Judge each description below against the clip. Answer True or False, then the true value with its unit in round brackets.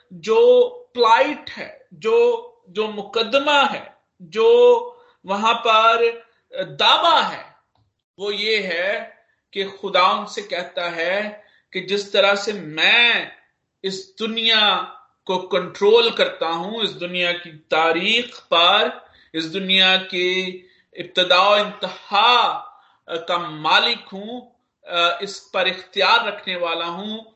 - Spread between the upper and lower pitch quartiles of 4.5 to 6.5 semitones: True (5.2 semitones)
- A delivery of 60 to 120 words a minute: True (110 wpm)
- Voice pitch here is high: True (205 Hz)